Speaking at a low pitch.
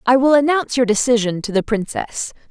No: high, 240 Hz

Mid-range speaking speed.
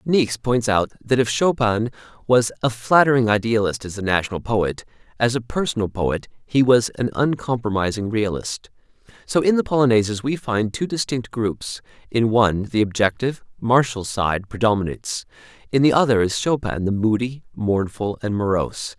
Yes: average, 155 wpm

